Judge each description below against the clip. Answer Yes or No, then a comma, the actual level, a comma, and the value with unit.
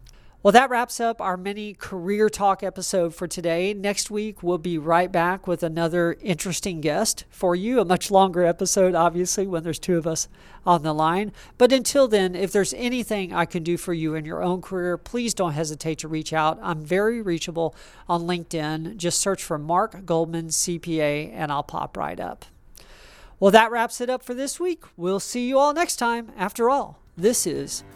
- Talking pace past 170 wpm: Yes, average, 195 wpm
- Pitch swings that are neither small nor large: Yes, average, 3.9 semitones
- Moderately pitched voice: Yes, medium, 180 Hz